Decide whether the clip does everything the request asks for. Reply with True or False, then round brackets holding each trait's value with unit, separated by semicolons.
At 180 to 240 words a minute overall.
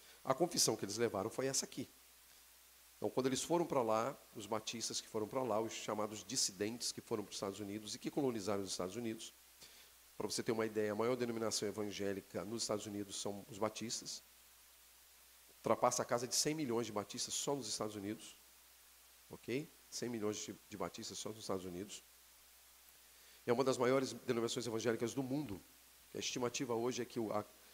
True (185 wpm)